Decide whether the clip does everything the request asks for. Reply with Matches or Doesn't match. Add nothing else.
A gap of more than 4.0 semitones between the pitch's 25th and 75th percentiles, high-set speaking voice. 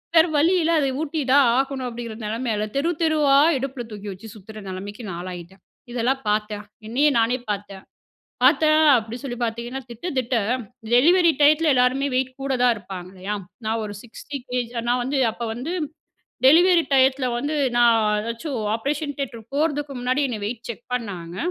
Matches